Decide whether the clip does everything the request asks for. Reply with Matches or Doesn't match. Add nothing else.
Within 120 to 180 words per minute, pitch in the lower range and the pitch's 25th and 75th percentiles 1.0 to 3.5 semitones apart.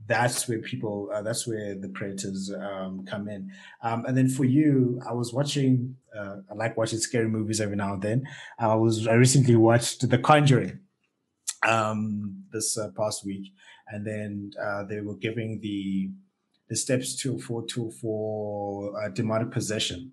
Matches